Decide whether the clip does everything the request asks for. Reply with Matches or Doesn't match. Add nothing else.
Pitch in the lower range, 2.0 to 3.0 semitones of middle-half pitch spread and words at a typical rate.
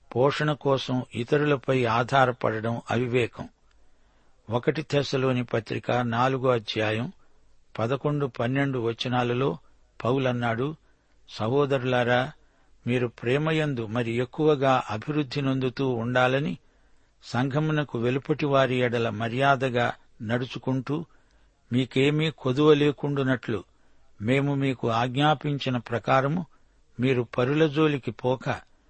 Matches